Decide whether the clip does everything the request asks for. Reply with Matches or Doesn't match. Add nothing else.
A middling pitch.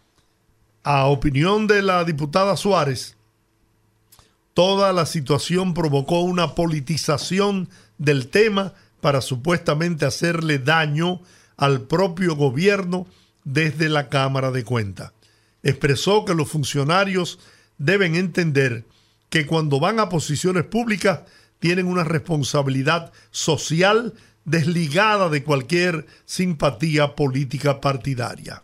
Matches